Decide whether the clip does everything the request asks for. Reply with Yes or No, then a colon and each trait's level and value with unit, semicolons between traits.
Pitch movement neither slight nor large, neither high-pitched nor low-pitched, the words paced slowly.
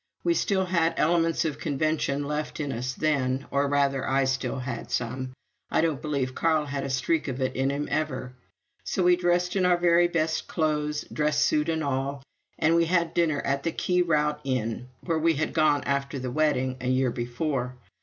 No: average, 3.6 semitones; medium, 150 Hz; average, 195 wpm